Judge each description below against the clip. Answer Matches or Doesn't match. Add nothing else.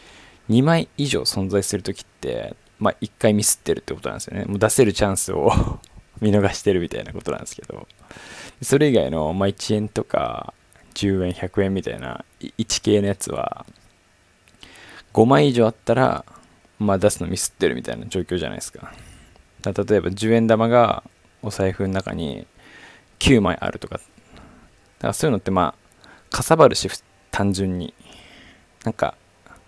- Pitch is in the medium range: Doesn't match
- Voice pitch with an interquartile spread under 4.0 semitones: Matches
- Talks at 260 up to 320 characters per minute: Matches